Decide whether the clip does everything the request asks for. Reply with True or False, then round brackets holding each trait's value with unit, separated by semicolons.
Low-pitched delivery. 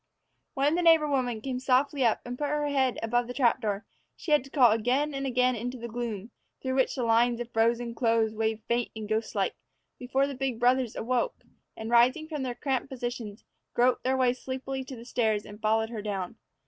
False (245 Hz)